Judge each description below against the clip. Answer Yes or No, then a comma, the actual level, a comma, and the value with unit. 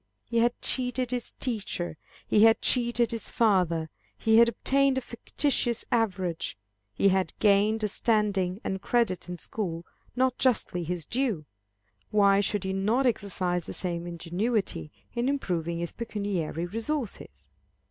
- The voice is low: No, high, 205 Hz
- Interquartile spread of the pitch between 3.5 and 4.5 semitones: No, average, 5.0 semitones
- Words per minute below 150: Yes, average, 140 wpm